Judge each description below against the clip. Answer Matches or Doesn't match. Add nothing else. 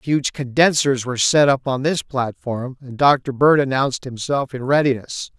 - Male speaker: Matches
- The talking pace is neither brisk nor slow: Matches